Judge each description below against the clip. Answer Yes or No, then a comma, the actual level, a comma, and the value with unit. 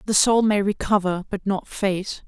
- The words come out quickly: No, average, 185 wpm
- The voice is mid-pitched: No, high, 200 Hz